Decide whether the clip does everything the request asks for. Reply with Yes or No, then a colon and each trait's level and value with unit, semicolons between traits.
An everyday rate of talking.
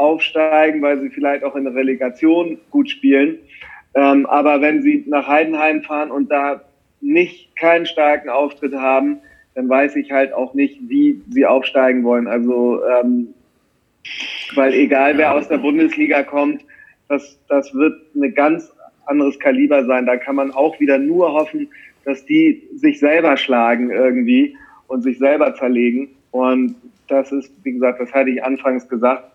Yes: average, 160 wpm